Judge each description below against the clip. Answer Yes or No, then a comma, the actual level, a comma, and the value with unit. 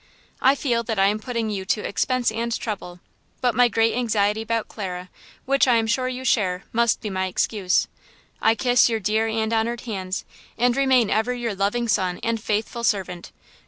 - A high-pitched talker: Yes, high, 225 Hz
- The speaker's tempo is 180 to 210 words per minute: Yes, average, 190 wpm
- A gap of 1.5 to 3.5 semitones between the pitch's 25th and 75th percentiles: Yes, average, 2.9 semitones